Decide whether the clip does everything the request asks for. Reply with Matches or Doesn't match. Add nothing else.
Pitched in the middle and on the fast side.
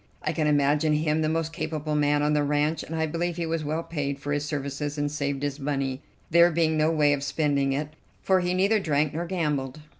Matches